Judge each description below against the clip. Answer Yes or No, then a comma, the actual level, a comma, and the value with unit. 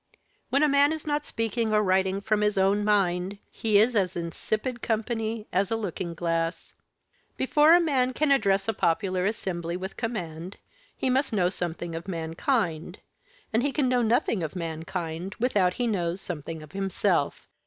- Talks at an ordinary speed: Yes, average, 170 wpm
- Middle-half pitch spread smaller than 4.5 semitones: No, average, 4.9 semitones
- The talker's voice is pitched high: Yes, high, 200 Hz